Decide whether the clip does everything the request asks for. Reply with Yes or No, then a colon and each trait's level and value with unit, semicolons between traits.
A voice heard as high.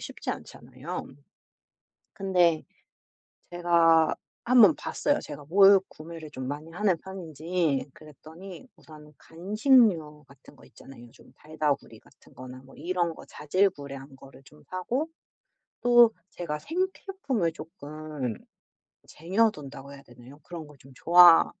No: medium, 165 Hz